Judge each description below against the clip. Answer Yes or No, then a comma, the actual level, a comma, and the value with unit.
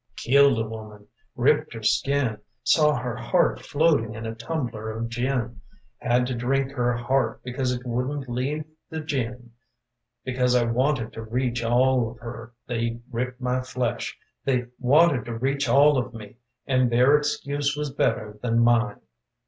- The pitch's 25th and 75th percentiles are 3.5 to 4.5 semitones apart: No, average, 2.7 semitones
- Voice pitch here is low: Yes, low, 125 Hz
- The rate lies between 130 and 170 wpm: Yes, average, 160 wpm